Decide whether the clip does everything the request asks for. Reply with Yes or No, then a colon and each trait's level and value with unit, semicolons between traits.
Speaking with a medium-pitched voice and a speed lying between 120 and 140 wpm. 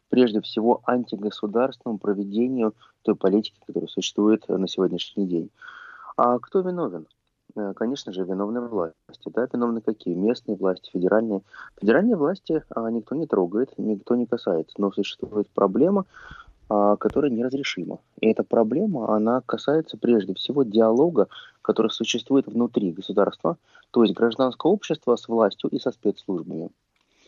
No: low, 110 Hz; average, 130 wpm